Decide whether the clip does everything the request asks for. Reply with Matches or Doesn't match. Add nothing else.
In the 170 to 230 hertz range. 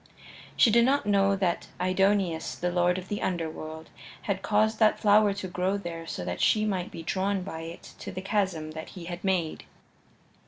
Matches